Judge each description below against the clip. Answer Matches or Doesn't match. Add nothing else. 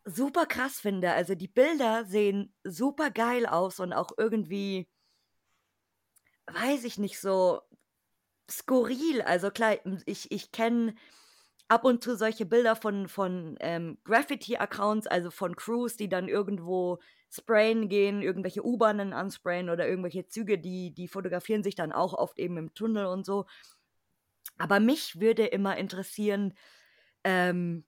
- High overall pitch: Matches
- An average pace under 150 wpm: Matches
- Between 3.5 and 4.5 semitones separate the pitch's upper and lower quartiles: Matches